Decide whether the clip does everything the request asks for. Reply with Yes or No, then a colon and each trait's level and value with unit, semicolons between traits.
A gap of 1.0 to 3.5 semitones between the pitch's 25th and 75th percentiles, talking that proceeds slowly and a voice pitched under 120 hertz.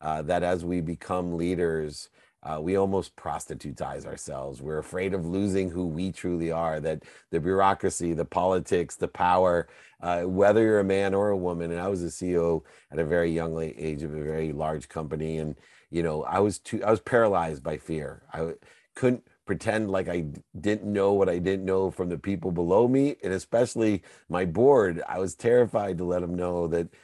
No: average, 2.9 semitones; average, 195 wpm; very low, 90 Hz